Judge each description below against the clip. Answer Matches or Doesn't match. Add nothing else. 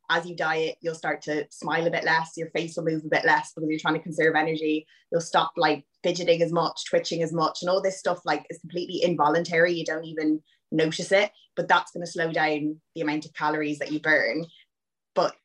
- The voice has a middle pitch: Matches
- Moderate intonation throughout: Doesn't match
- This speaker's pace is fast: Matches